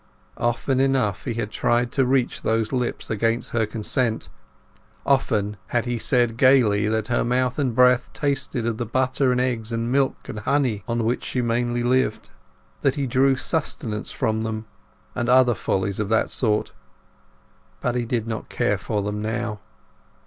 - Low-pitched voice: Yes, low, 120 Hz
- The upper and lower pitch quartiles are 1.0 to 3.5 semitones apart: Yes, narrow, 2.6 semitones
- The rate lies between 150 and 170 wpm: Yes, average, 165 wpm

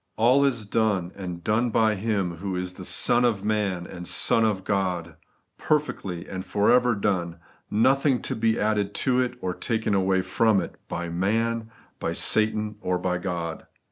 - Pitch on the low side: Yes, low, 105 Hz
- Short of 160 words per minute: No, average, 165 wpm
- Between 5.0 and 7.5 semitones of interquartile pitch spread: No, average, 3.7 semitones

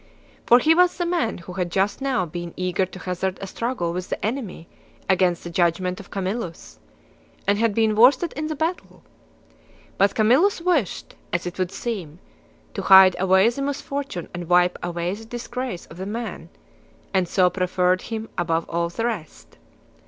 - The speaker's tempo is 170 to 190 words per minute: Yes, average, 175 wpm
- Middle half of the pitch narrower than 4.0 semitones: No, average, 5.1 semitones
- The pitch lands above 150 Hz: Yes, high, 190 Hz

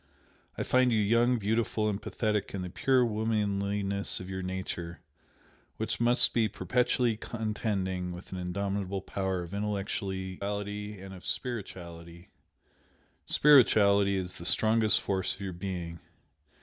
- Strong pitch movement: No, average, 2.7 semitones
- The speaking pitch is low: Yes, low, 100 Hz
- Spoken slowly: Yes, slow, 130 wpm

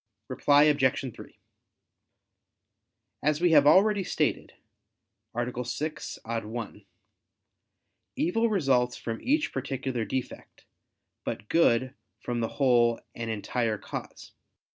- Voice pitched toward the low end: Yes, low, 130 Hz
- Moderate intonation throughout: Yes, average, 4.4 semitones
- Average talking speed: No, slow, 105 wpm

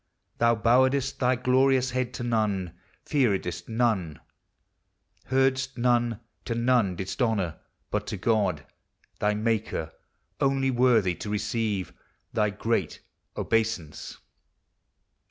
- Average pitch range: Yes, average, 3.9 semitones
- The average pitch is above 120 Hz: No, low, 115 Hz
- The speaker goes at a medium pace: No, slow, 105 wpm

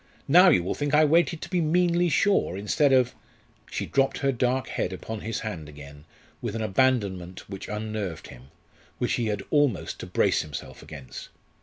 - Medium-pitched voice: No, low, 115 Hz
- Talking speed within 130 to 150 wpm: No, average, 185 wpm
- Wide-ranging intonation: Yes, wide, 7.6 semitones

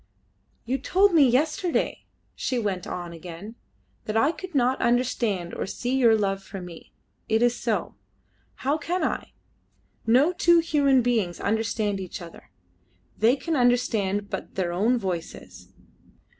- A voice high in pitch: Yes, high, 235 Hz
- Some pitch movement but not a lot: No, wide, 5.7 semitones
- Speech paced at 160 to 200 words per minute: No, average, 145 wpm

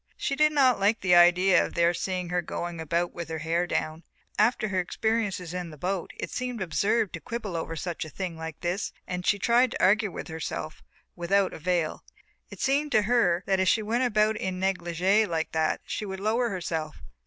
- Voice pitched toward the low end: No, medium, 185 Hz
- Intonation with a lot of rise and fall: No, average, 4.0 semitones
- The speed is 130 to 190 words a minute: No, average, 200 wpm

